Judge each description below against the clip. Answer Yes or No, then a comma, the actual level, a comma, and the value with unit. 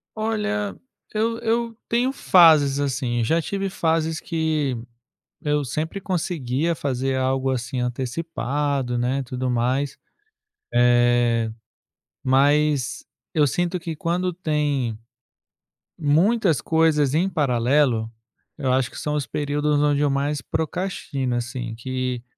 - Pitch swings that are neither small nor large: Yes, average, 4.4 semitones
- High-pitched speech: No, medium, 145 Hz